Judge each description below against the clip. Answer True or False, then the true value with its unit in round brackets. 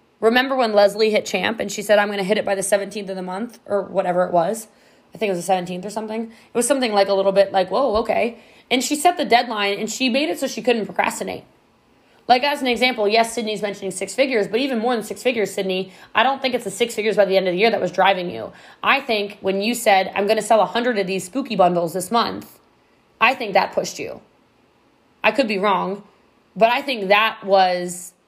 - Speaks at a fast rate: True (250 wpm)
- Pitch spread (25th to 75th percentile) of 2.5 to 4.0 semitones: True (3.4 semitones)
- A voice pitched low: False (210 Hz)